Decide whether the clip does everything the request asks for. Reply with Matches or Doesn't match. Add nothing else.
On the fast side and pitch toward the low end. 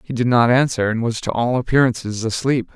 Matches